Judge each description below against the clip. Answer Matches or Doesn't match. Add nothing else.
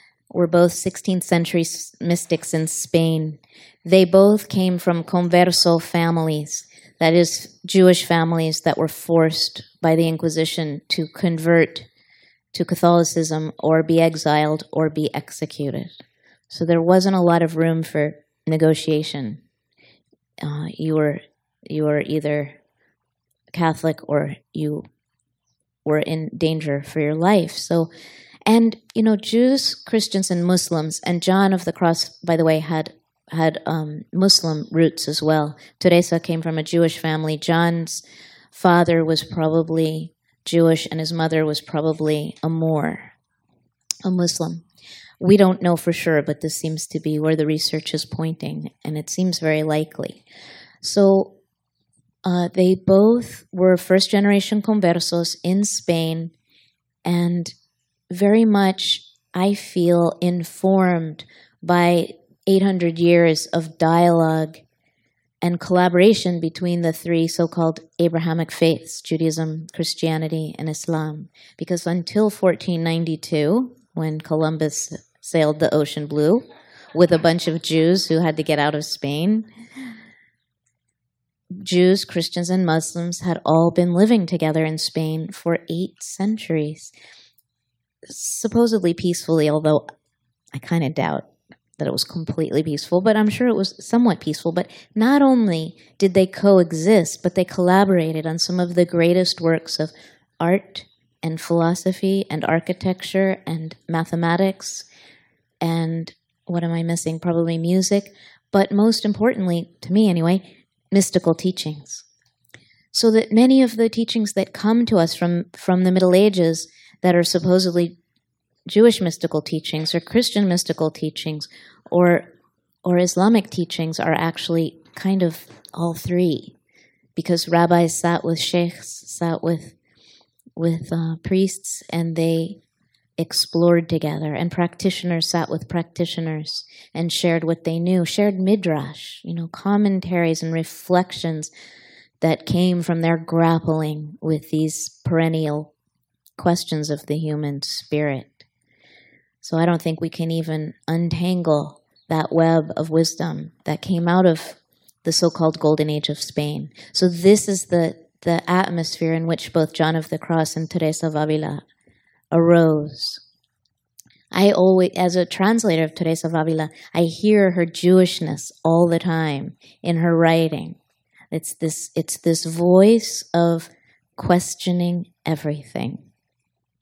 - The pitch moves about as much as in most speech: Doesn't match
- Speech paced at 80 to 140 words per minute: Matches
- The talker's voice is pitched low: Doesn't match